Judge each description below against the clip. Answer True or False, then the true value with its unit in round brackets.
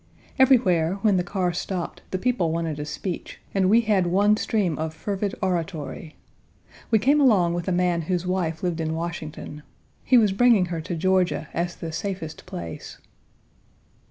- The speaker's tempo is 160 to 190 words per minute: True (165 wpm)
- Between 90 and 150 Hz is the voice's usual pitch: False (180 Hz)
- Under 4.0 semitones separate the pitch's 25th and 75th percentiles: True (3.4 semitones)